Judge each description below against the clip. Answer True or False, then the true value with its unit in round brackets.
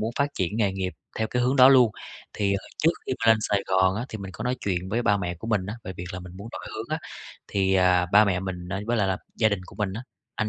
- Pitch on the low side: True (100 Hz)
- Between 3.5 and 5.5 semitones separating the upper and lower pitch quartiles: False (3.1 semitones)